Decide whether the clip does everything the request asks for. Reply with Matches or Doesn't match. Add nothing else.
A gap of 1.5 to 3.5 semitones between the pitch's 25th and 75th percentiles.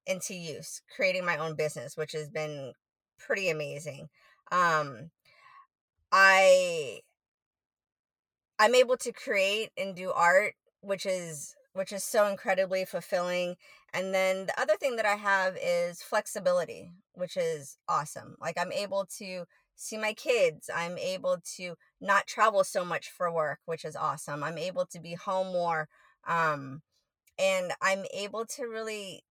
Doesn't match